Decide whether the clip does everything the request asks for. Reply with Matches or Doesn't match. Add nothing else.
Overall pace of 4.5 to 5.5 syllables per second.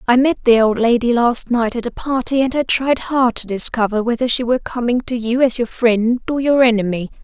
Matches